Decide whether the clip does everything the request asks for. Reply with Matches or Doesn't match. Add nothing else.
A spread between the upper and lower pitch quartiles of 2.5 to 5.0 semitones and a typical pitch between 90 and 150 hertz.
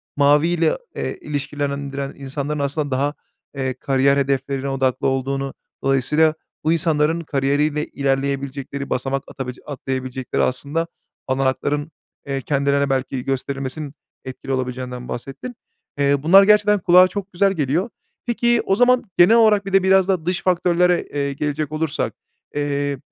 Matches